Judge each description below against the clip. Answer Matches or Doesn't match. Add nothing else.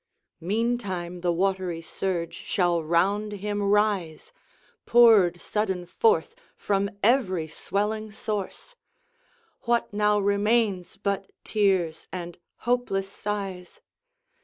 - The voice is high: Matches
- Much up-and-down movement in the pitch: Doesn't match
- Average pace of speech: Doesn't match